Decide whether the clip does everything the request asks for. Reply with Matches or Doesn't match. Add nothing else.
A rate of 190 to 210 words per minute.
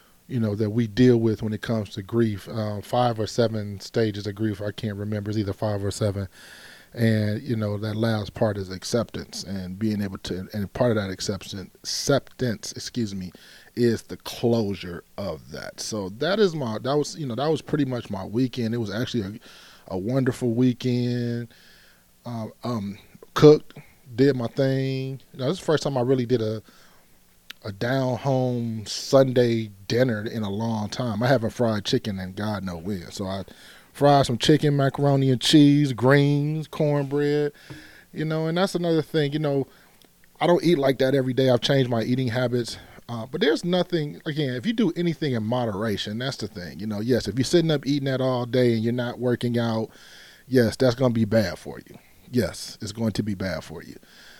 Matches